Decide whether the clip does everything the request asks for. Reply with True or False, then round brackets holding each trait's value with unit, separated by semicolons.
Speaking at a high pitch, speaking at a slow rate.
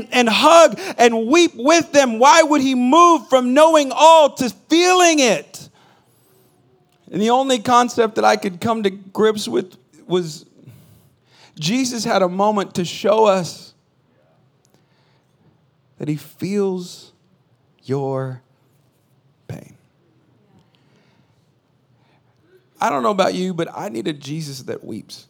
True (195 Hz; 125 wpm)